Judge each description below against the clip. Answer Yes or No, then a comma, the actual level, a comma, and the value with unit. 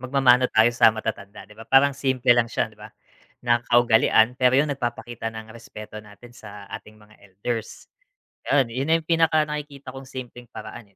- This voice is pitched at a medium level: No, low, 120 Hz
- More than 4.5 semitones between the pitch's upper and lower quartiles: No, average, 3.3 semitones